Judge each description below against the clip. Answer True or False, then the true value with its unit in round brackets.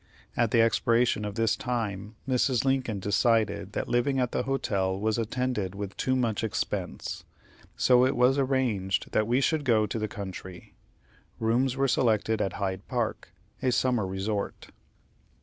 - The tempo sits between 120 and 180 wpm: True (155 wpm)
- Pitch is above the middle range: False (115 Hz)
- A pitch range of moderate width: True (3.7 semitones)